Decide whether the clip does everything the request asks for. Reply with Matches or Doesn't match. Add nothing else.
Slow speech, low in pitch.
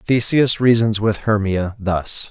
Matches